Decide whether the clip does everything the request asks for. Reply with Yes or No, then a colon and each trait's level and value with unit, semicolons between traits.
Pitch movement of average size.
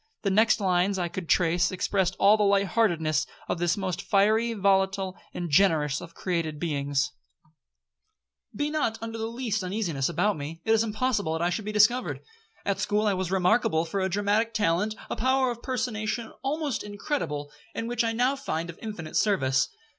Yes: average, 4.4 semitones